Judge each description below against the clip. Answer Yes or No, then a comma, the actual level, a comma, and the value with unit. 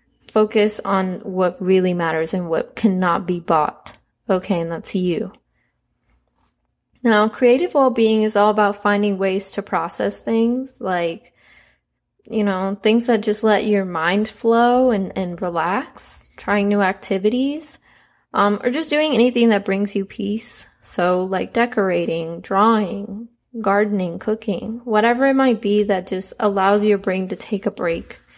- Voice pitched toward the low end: No, high, 205 Hz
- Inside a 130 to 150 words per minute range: Yes, average, 145 wpm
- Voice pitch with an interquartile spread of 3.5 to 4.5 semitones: No, average, 3.1 semitones